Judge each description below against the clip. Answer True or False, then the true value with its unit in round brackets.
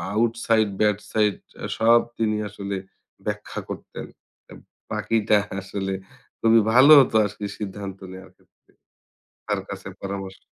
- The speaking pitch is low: True (105 Hz)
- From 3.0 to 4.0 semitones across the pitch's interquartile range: False (2.4 semitones)